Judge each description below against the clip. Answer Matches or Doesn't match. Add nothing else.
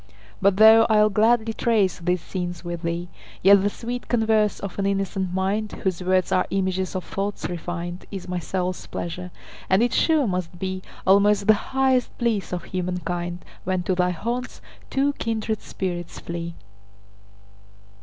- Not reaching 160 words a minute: Matches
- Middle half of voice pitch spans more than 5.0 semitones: Doesn't match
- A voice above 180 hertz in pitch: Matches